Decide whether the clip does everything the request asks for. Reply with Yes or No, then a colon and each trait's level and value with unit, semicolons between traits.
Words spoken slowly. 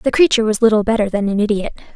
No: fast, 245 wpm